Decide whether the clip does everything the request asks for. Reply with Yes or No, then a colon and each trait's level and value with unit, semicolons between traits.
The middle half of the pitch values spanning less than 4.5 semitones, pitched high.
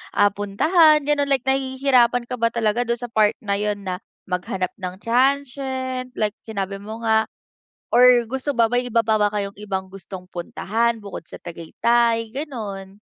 Yes: average, 4.0 semitones; high, 230 Hz